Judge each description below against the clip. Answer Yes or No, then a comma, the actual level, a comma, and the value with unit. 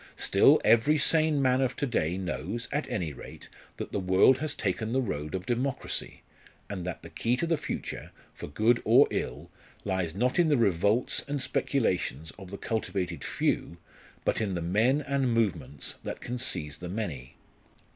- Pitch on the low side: Yes, low, 110 Hz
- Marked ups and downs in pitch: Yes, wide, 6.3 semitones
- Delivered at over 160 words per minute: Yes, average, 175 wpm